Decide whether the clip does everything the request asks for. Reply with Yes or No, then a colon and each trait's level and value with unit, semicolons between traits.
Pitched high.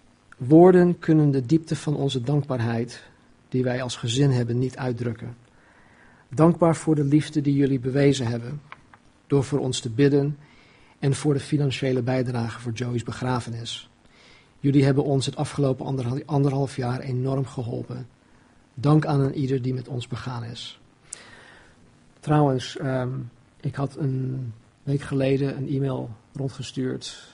No: low, 135 Hz